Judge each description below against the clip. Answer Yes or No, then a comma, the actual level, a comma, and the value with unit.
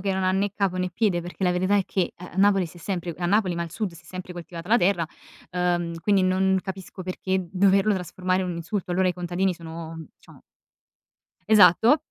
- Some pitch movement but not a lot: No, narrow, 1.7 semitones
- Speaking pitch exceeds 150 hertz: Yes, medium, 185 Hz